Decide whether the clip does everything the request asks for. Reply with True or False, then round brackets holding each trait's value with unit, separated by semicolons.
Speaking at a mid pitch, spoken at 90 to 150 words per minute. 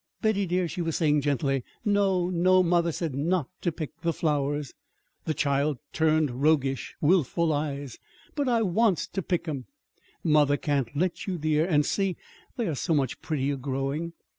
False (155 Hz; 165 wpm)